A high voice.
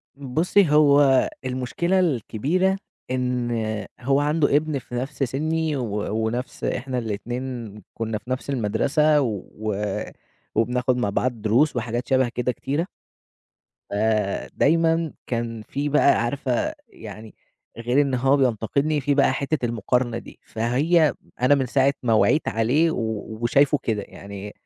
No: low, 130 Hz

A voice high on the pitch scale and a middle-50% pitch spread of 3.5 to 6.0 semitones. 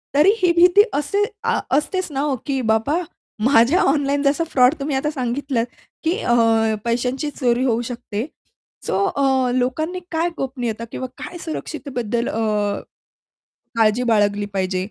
Yes: very high, 265 Hz; average, 4.3 semitones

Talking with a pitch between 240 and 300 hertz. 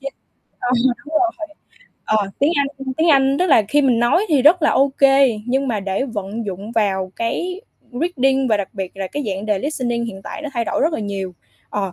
Yes: high, 245 Hz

